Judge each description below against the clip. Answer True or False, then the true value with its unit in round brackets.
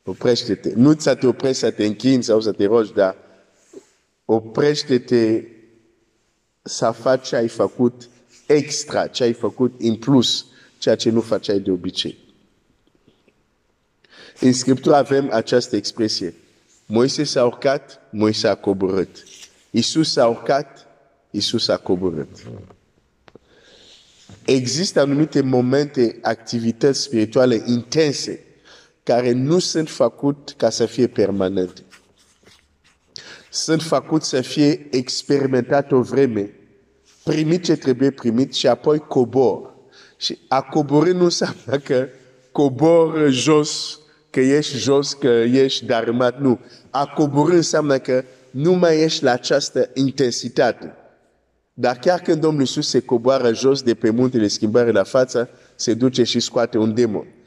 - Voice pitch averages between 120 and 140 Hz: True (130 Hz)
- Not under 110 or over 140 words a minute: True (125 wpm)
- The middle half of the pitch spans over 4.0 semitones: False (3.7 semitones)